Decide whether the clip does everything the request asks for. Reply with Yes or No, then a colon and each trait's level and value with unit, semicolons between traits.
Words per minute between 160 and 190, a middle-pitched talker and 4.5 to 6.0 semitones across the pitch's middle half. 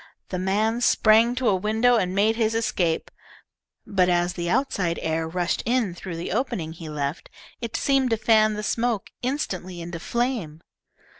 No: average, 165 wpm; high, 200 Hz; average, 4.9 semitones